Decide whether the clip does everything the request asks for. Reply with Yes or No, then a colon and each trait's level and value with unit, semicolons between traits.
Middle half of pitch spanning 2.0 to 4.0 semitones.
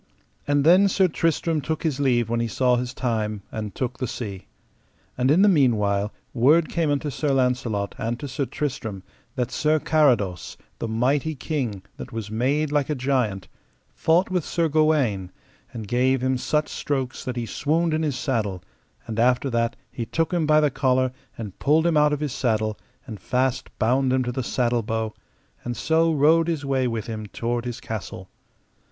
No: average, 4.7 semitones